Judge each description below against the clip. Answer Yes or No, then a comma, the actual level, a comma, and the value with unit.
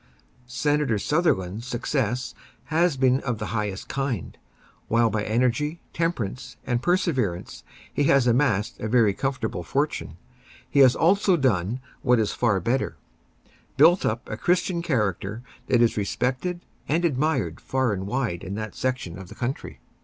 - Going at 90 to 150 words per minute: Yes, average, 145 wpm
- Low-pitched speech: Yes, low, 125 Hz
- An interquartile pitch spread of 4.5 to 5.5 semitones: Yes, average, 5.2 semitones